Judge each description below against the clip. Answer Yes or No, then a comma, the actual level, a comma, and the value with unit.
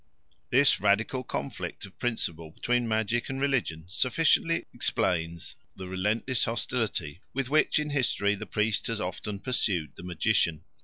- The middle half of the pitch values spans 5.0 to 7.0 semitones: Yes, wide, 5.6 semitones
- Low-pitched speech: Yes, low, 105 Hz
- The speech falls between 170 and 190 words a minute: No, average, 140 wpm